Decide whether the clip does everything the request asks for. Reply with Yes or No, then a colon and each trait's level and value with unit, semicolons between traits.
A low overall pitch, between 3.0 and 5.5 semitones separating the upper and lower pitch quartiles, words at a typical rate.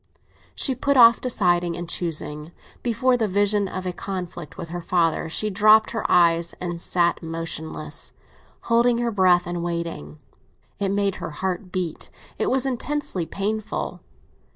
No: medium, 185 Hz; average, 4.3 semitones; average, 150 wpm